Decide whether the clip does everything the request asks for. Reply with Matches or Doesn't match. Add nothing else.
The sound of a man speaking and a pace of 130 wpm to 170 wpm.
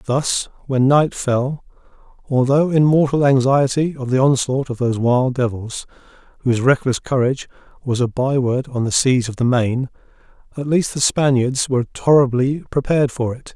Matches